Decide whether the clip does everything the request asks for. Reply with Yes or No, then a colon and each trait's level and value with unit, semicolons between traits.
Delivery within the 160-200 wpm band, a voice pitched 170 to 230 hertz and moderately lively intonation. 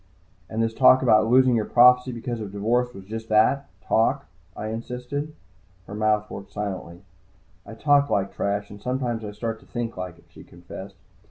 No: average, 180 wpm; low, 115 Hz; average, 3.2 semitones